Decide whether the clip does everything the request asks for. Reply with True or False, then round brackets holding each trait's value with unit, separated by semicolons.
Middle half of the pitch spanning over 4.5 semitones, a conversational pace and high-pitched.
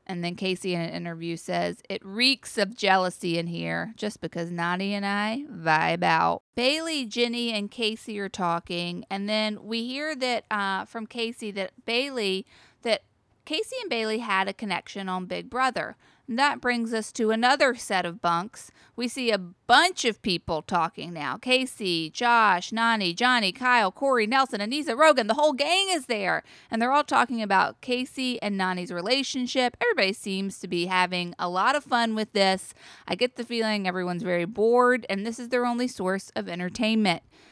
True (5.0 semitones; 180 wpm; 215 Hz)